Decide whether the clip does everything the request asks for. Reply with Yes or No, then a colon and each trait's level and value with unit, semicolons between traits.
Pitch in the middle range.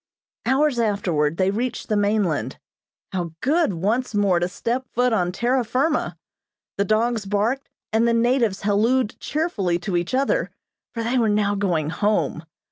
No: high, 215 Hz